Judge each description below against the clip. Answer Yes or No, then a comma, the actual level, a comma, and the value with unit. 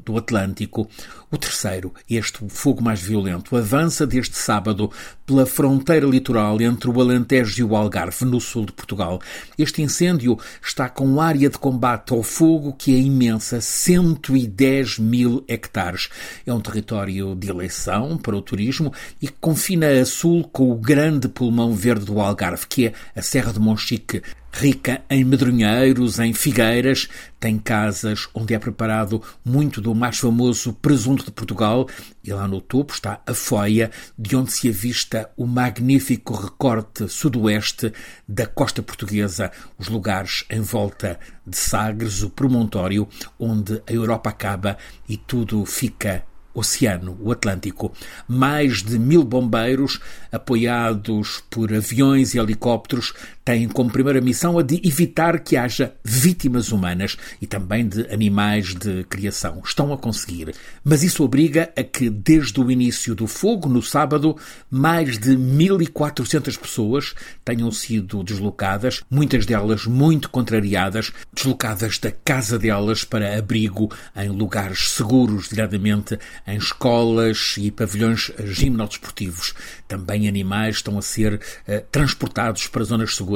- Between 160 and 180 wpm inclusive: No, average, 140 wpm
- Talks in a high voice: No, low, 115 Hz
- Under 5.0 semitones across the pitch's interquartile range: Yes, average, 3.9 semitones